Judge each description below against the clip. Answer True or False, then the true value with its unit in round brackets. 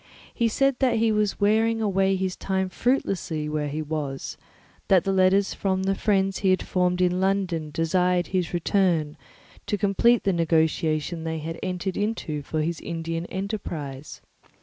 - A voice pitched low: False (185 Hz)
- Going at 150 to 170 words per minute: True (155 wpm)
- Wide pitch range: False (3.4 semitones)